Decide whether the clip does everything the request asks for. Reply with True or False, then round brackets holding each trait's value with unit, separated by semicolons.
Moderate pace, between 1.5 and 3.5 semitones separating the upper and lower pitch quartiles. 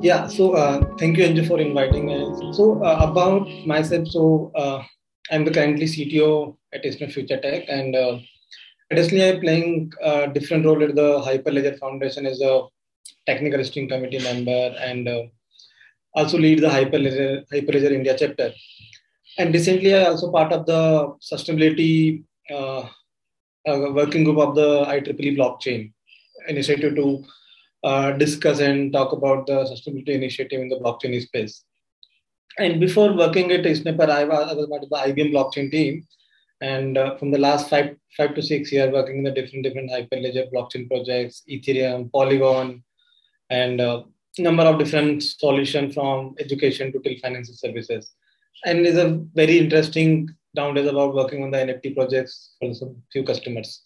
True (160 wpm; 2.9 semitones)